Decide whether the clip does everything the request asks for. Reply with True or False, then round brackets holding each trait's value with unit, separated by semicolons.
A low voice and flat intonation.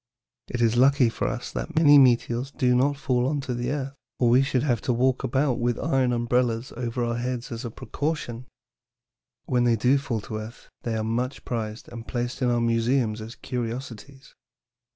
True (125 Hz; 2.2 semitones)